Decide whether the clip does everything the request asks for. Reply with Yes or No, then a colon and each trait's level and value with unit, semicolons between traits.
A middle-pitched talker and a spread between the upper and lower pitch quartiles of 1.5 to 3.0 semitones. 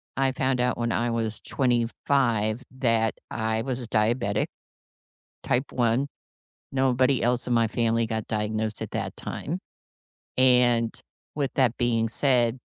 No: low, 120 Hz; narrow, 2.4 semitones